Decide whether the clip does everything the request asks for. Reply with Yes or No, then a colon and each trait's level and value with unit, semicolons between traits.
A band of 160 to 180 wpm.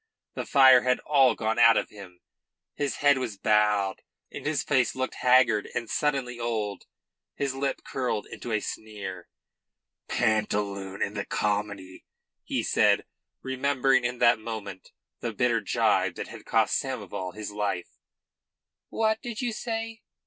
No: average, 145 wpm